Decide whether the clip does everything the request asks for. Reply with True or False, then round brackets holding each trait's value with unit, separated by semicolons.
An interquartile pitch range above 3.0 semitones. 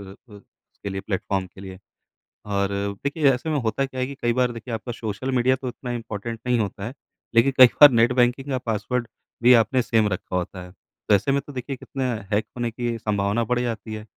True (3.6 semitones)